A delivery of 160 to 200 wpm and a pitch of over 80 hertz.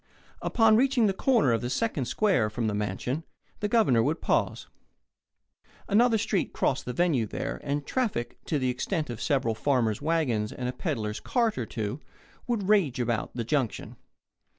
Yes: average, 170 wpm; medium, 140 Hz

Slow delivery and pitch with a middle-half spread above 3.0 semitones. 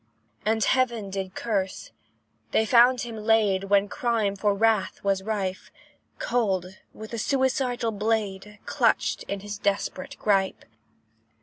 No: slow, 125 wpm; narrow, 2.5 semitones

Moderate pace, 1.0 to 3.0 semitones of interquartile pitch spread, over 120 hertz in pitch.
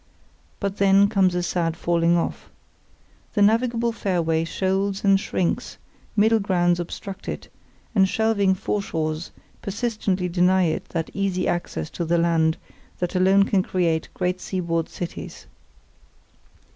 No: slow, 130 wpm; narrow, 2.6 semitones; medium, 185 Hz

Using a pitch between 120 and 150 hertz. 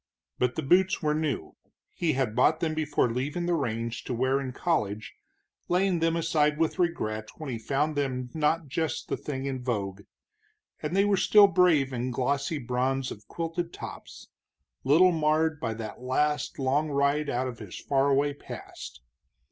Yes: medium, 140 Hz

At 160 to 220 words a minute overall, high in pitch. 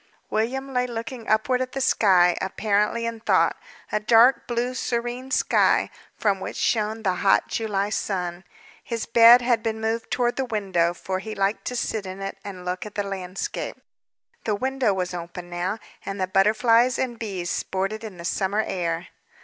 Yes: average, 175 wpm; high, 215 Hz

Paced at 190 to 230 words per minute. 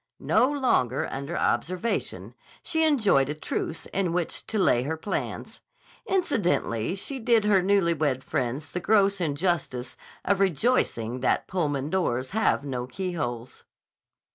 No: slow, 135 wpm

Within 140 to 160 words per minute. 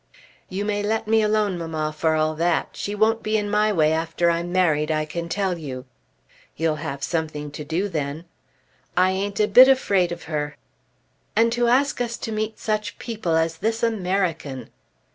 No: average, 180 wpm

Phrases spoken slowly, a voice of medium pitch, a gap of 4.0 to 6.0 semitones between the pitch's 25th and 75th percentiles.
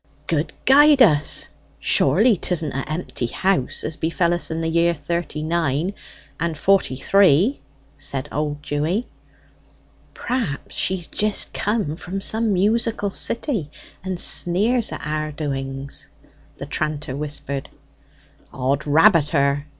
Yes: slow, 125 wpm; medium, 165 Hz; average, 5.1 semitones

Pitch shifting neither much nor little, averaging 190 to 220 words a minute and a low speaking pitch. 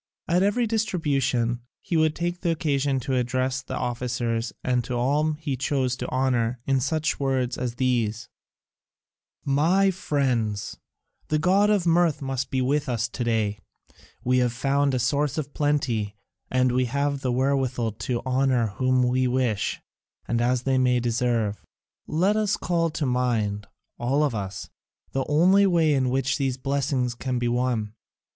No: average, 3.4 semitones; average, 160 wpm; low, 130 Hz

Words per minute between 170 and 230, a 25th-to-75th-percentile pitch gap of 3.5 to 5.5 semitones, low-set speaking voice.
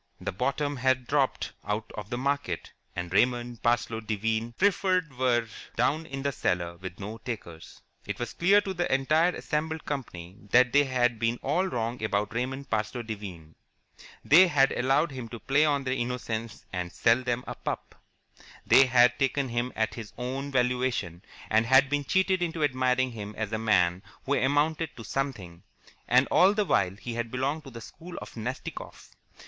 Yes: average, 175 wpm; average, 4.0 semitones; low, 125 Hz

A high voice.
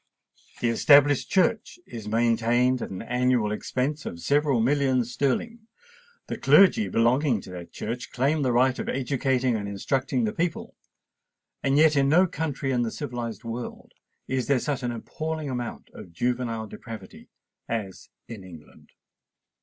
No: low, 125 Hz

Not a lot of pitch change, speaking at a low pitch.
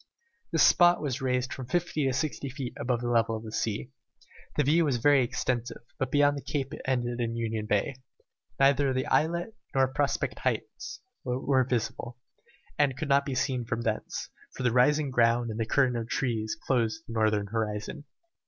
No: average, 3.3 semitones; low, 125 Hz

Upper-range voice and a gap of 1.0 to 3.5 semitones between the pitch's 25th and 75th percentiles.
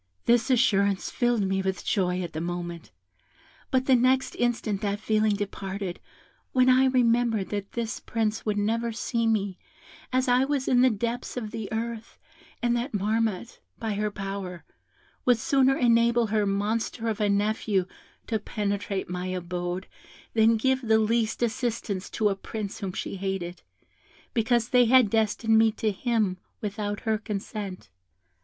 Yes: high, 220 Hz; average, 3.0 semitones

